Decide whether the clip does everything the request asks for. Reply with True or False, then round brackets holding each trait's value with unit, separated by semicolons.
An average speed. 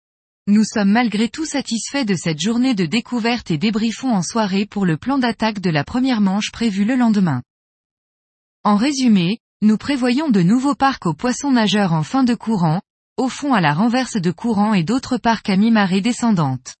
True (185 wpm)